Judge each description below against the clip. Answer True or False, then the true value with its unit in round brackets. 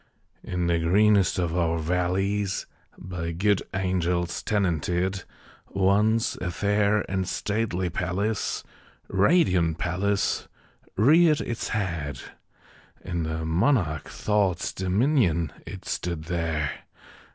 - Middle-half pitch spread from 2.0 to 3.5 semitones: True (3.2 semitones)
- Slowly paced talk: True (100 wpm)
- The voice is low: True (95 Hz)